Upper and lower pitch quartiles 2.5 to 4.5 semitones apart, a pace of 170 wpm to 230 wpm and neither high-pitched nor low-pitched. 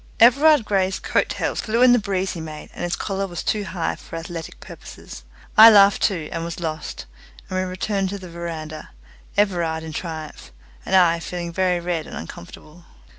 Yes: average, 3.3 semitones; average, 185 wpm; medium, 175 Hz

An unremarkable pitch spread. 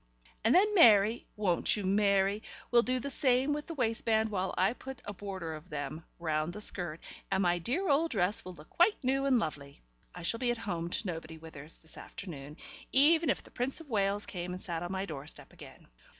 No: wide, 6.6 semitones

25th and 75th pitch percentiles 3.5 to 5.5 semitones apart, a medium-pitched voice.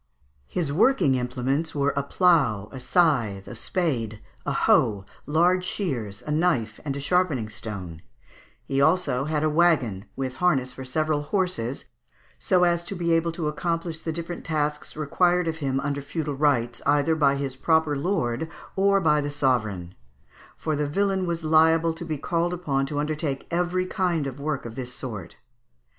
Yes: average, 4.6 semitones; medium, 150 Hz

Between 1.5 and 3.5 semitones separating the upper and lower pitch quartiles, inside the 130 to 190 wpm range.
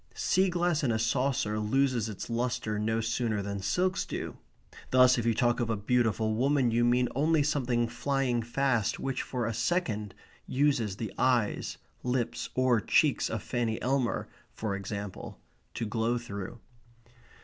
Yes: average, 3.0 semitones; average, 155 wpm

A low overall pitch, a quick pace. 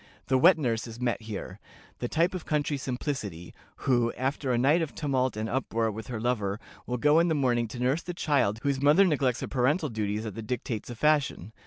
Yes: low, 125 Hz; fast, 215 wpm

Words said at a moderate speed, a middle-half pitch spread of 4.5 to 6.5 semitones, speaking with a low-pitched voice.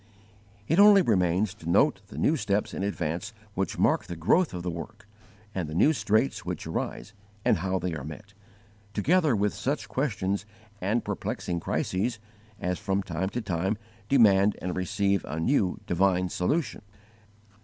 No: average, 160 wpm; average, 3.5 semitones; low, 100 Hz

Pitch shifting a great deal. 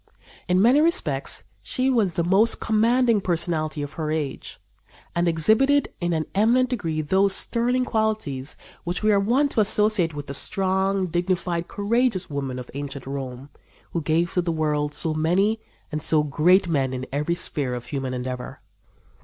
Yes: wide, 6.4 semitones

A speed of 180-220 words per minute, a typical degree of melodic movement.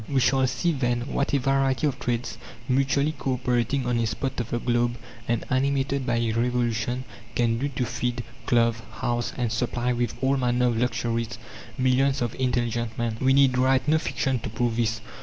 No: average, 185 wpm; narrow, 2.0 semitones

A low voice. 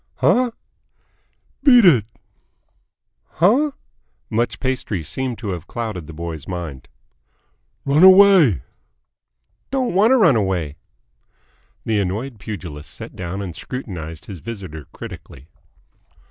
Yes: low, 105 Hz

